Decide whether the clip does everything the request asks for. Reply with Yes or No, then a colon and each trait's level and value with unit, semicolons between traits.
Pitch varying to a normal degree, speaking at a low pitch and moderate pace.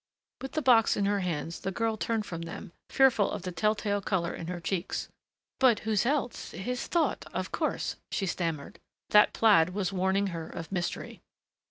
No: average, 4.3 semitones; high, 200 Hz; average, 185 wpm